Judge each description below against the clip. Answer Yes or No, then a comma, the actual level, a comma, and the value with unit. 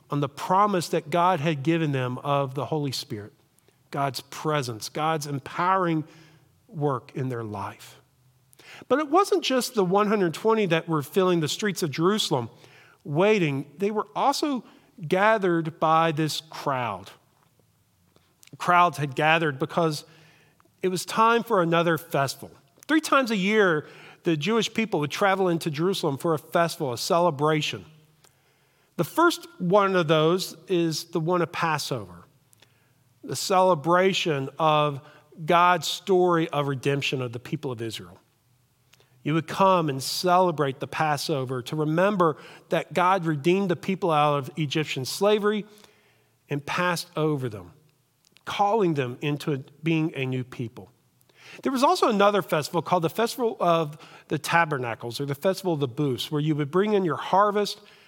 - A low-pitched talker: No, medium, 160 Hz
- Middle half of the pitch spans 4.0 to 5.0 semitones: Yes, average, 4.5 semitones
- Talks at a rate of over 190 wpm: No, average, 145 wpm